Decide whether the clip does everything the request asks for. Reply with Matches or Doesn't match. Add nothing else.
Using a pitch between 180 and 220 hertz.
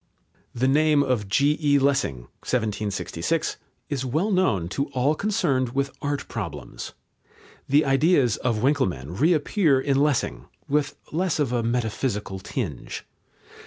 Doesn't match